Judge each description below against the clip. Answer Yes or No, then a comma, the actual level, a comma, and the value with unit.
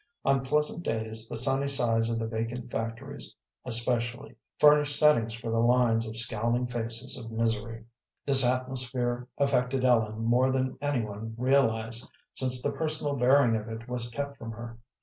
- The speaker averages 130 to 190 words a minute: Yes, average, 155 wpm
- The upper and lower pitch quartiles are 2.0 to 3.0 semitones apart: Yes, narrow, 2.5 semitones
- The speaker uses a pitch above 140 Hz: No, low, 120 Hz